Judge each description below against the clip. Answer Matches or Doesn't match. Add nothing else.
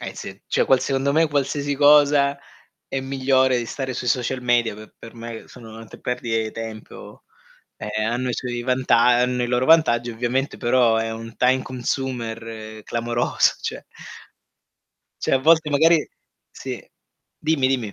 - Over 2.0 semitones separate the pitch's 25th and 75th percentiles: Matches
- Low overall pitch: Matches